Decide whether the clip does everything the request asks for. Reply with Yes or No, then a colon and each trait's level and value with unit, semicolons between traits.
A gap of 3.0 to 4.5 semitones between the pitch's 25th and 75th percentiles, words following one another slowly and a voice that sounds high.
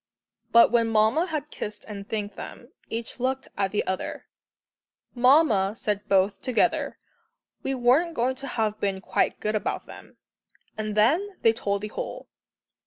No: average, 4.0 semitones; average, 155 wpm; high, 225 Hz